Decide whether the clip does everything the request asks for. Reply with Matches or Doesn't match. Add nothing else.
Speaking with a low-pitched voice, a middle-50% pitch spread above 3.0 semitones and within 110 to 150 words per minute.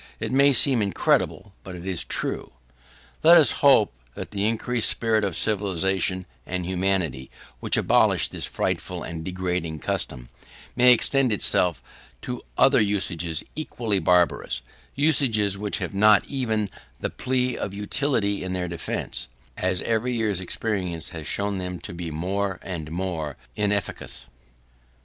Matches